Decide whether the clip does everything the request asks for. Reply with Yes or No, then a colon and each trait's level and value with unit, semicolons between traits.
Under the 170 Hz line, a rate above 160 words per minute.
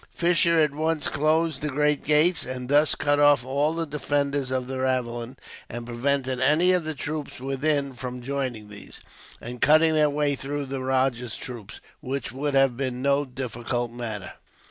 Yes: medium, 140 Hz; average, 170 wpm